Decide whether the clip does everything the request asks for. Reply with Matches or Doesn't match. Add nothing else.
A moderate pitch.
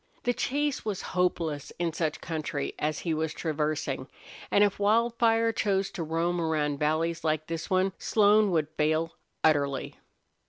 Matches